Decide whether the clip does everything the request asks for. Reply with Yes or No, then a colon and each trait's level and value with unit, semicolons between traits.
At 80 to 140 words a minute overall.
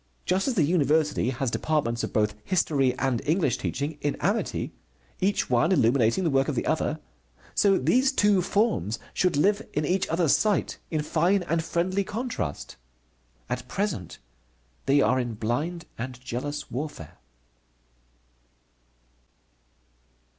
Yes: slow, 135 wpm